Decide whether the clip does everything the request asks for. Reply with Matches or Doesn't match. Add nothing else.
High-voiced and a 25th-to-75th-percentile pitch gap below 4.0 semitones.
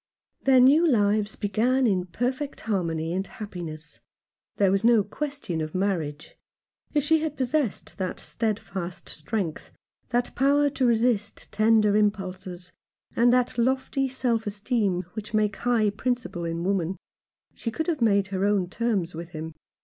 Doesn't match